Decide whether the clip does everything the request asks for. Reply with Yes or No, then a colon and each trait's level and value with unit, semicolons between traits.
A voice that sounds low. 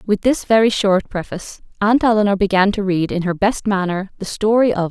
No: high, 200 Hz